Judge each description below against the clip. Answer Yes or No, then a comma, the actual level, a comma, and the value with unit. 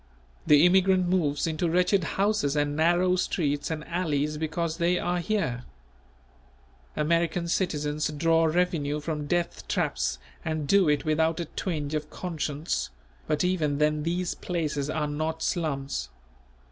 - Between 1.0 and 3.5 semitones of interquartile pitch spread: Yes, average, 2.9 semitones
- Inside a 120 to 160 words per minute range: Yes, slow, 135 wpm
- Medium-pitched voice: Yes, medium, 160 Hz